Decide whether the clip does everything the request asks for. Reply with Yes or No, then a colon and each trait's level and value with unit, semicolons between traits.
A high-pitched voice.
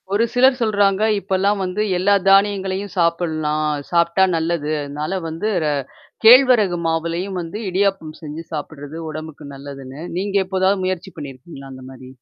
No: medium, 175 Hz